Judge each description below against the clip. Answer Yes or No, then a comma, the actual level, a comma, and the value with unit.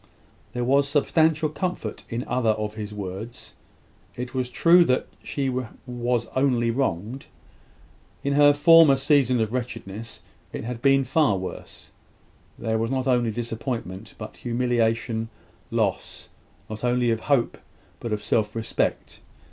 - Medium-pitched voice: No, low, 120 Hz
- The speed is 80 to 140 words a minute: Yes, slow, 135 wpm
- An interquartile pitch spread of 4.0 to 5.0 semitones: No, average, 3.3 semitones